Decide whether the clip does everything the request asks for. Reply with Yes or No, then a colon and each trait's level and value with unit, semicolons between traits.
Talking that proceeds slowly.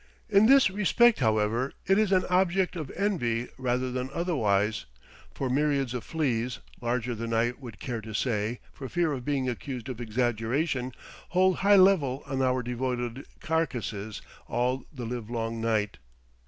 No: average, 155 wpm